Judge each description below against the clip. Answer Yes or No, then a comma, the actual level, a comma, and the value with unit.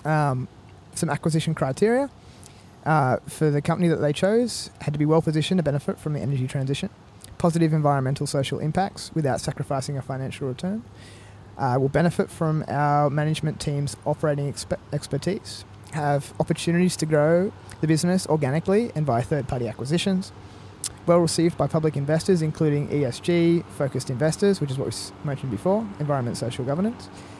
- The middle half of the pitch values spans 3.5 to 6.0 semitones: Yes, average, 3.8 semitones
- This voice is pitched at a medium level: Yes, medium, 150 Hz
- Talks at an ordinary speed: Yes, average, 150 wpm